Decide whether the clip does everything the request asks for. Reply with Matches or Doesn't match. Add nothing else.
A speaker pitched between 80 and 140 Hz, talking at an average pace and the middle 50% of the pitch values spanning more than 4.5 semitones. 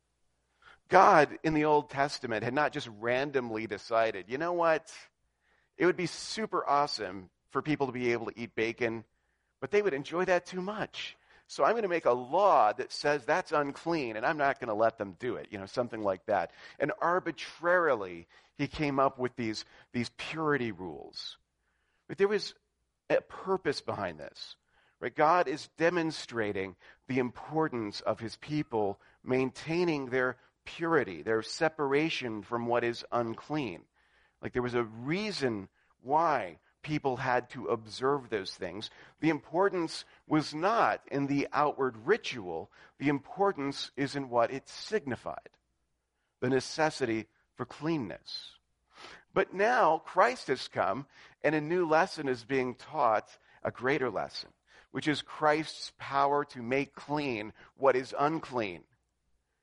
Matches